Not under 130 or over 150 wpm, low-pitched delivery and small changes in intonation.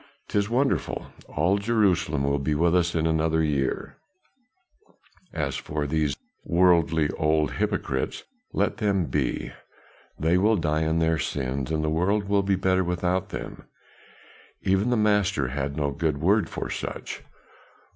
No: average, 145 wpm; very low, 80 Hz; average, 4.2 semitones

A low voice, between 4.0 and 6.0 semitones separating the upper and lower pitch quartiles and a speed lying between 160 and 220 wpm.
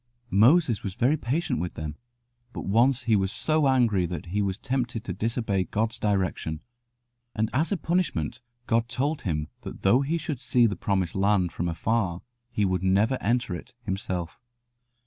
Yes: low, 110 Hz; average, 5.2 semitones; average, 170 wpm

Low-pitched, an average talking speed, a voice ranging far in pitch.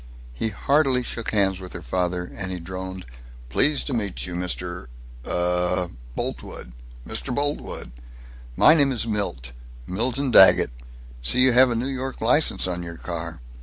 Yes: very low, 95 Hz; average, 155 wpm; wide, 6.1 semitones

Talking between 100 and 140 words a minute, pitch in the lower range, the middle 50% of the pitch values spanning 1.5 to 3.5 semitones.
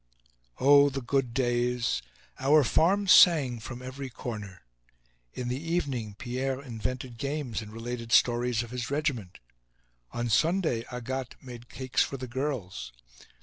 Yes: slow, 135 wpm; low, 125 Hz; average, 2.7 semitones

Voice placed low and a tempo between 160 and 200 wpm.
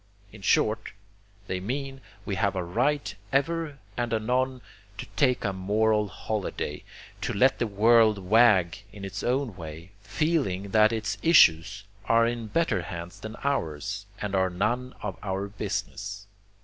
No: low, 105 Hz; average, 150 wpm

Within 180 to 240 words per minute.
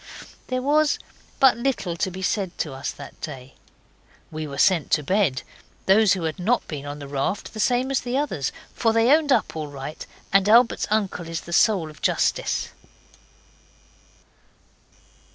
No: average, 160 wpm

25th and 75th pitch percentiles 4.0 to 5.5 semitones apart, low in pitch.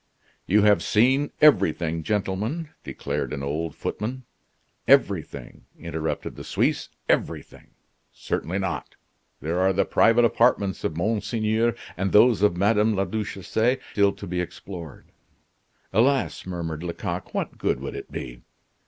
Yes: average, 4.7 semitones; low, 100 Hz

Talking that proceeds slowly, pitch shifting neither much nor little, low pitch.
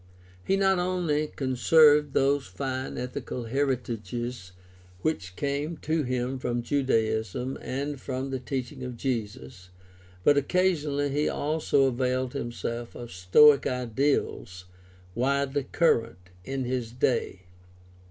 Yes: slow, 115 wpm; average, 3.2 semitones; low, 130 Hz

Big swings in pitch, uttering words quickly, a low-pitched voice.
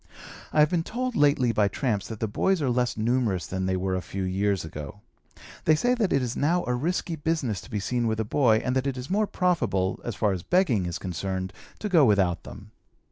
Yes: wide, 7.8 semitones; fast, 235 wpm; low, 120 Hz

